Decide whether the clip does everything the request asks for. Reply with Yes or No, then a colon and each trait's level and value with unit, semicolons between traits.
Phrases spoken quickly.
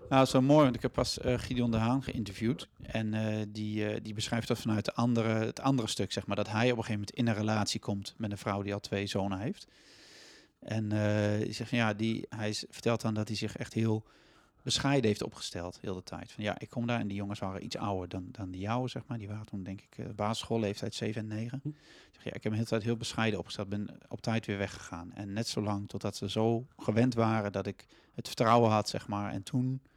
Yes: fast, 260 wpm